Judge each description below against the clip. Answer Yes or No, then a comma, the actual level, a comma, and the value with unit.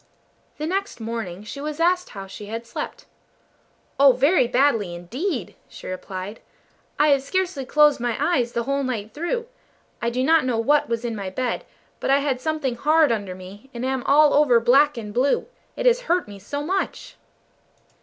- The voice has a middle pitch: No, very high, 260 Hz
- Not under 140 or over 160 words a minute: No, average, 185 wpm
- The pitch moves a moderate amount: Yes, average, 4.8 semitones